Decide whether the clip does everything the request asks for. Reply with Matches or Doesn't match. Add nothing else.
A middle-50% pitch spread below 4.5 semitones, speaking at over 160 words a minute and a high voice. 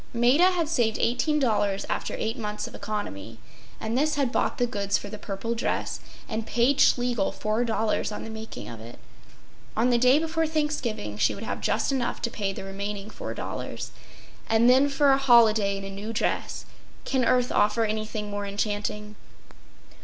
Matches